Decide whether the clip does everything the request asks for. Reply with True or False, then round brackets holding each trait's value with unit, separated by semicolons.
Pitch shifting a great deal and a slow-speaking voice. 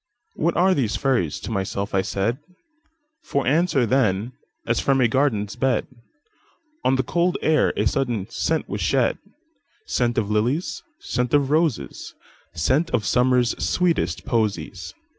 True (6.9 semitones; 125 wpm)